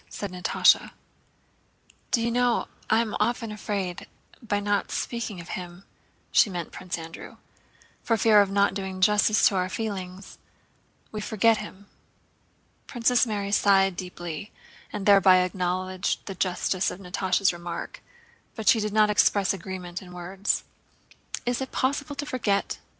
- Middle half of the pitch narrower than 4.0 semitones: Yes, average, 2.8 semitones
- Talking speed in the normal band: Yes, average, 145 wpm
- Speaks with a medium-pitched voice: No, high, 200 Hz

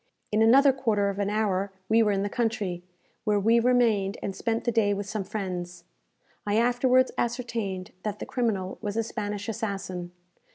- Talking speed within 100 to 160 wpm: No, average, 175 wpm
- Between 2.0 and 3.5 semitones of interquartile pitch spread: Yes, average, 2.8 semitones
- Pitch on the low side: No, high, 210 Hz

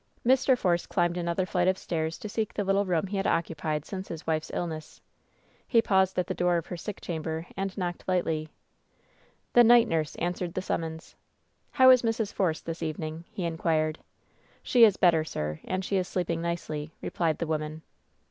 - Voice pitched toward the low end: No, medium, 175 Hz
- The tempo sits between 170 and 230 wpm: Yes, average, 190 wpm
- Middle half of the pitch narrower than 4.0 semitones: Yes, average, 3.1 semitones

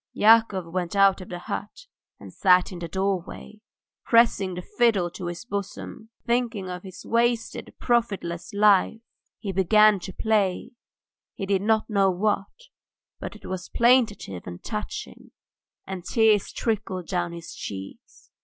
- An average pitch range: Yes, average, 3.5 semitones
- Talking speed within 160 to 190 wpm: No, average, 145 wpm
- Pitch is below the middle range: No, high, 195 Hz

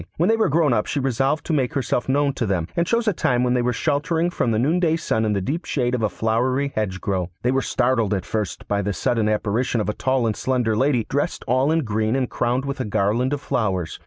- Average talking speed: No, fast, 250 wpm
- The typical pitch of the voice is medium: No, low, 125 Hz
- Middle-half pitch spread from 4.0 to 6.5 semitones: Yes, average, 4.7 semitones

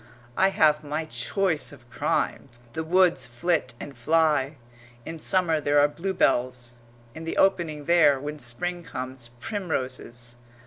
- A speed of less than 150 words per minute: Yes, slow, 135 wpm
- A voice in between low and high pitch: Yes, medium, 150 Hz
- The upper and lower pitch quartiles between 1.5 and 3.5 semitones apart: No, average, 4.9 semitones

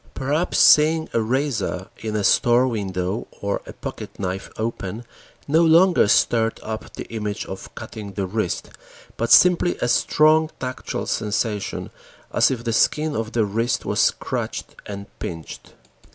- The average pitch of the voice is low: Yes, low, 115 Hz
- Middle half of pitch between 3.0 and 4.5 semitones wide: No, wide, 5.5 semitones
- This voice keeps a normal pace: Yes, average, 150 wpm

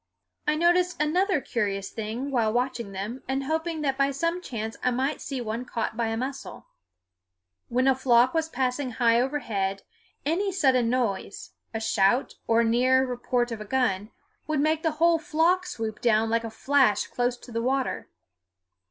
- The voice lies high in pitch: Yes, very high, 255 Hz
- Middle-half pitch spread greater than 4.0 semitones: Yes, average, 4.6 semitones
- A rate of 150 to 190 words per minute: Yes, average, 175 wpm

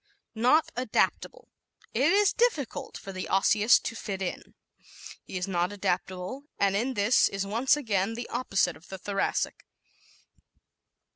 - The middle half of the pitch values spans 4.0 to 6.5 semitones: Yes, average, 5.0 semitones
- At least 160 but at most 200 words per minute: No, average, 145 wpm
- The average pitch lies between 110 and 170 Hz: No, high, 205 Hz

